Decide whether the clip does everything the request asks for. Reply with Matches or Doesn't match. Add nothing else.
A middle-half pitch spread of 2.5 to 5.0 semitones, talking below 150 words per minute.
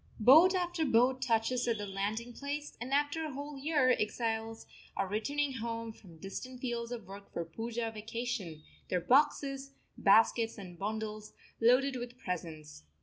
Doesn't match